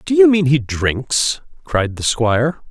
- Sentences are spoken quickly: No, average, 180 wpm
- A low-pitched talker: Yes, low, 130 Hz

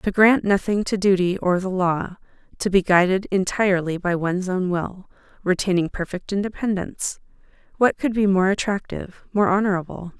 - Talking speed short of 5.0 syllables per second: No, 5.3 syllables/s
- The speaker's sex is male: No, female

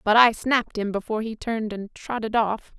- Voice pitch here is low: No, high, 220 Hz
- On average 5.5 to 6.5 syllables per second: Yes, 5.7 syllables/s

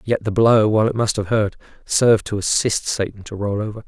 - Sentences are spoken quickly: Yes, fast, 230 wpm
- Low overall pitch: Yes, low, 105 Hz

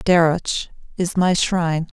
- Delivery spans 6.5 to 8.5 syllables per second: No, 4.7 syllables/s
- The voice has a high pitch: No, medium, 170 Hz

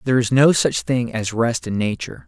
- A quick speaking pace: Yes, fast, 235 wpm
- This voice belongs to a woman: No, male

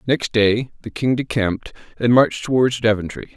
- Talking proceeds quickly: No, average, 160 wpm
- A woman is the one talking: No, male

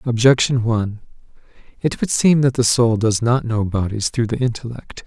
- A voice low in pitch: Yes, low, 120 Hz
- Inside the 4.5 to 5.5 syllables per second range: Yes, 5.0 syllables/s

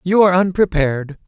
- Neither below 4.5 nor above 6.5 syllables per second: Yes, 6.3 syllables/s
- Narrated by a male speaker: Yes, male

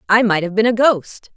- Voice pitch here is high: Yes, high, 210 Hz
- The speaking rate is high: Yes, fast, 265 wpm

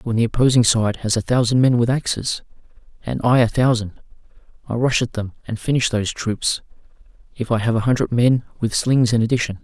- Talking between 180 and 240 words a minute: Yes, average, 200 wpm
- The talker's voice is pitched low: Yes, low, 115 Hz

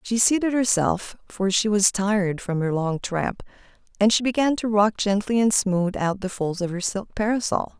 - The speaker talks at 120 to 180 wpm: No, average, 200 wpm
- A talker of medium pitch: No, high, 205 Hz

